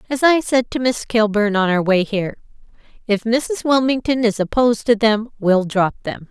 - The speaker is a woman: Yes, female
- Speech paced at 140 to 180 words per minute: No, average, 190 wpm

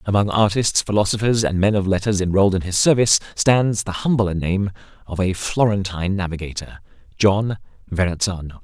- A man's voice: Yes, male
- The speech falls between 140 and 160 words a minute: Yes, average, 145 wpm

